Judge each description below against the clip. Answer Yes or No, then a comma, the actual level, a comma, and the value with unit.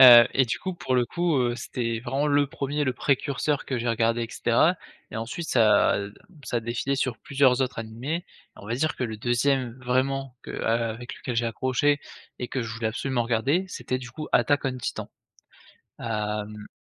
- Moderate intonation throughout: Yes, average, 3.0 semitones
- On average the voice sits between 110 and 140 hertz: Yes, low, 125 Hz